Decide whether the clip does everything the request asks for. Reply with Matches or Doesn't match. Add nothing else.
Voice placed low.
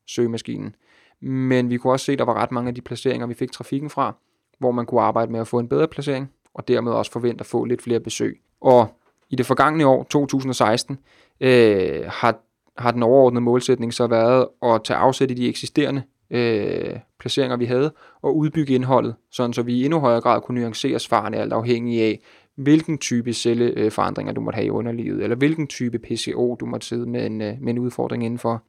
Matches